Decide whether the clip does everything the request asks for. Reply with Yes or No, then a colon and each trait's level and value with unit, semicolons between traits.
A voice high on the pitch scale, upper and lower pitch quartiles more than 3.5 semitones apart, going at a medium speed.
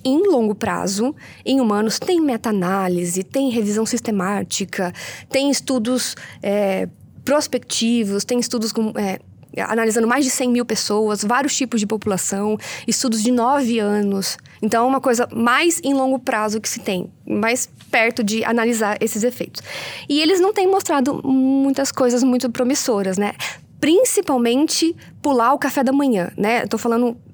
Yes: high, 235 Hz; average, 4.1 semitones; average, 150 wpm